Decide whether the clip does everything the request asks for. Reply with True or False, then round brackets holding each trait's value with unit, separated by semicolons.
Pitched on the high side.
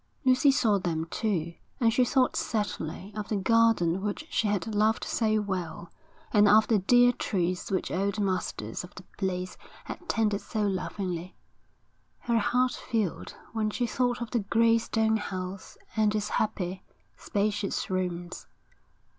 True (210 Hz)